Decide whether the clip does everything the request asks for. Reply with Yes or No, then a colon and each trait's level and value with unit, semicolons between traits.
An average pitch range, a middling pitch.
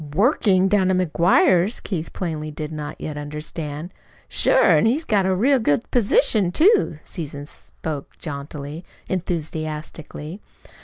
Yes: average, 4.8 semitones; medium, 170 Hz